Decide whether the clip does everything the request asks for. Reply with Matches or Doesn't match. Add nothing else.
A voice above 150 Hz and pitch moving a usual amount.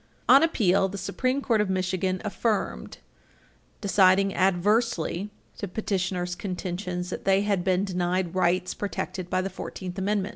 Doesn't match